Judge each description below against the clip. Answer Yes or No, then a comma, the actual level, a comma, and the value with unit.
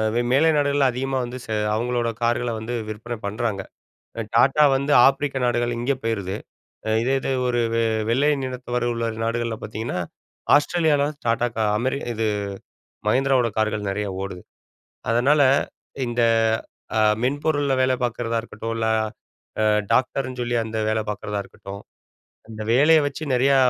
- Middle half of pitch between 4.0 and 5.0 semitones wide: No, average, 3.2 semitones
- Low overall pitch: Yes, low, 120 Hz